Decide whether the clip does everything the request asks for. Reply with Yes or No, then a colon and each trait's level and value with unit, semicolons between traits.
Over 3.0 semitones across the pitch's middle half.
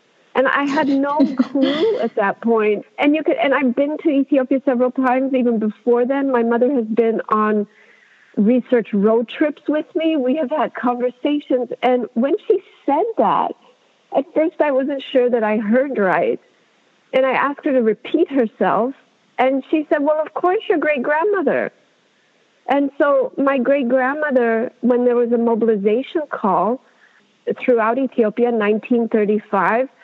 Yes: average, 4.0 semitones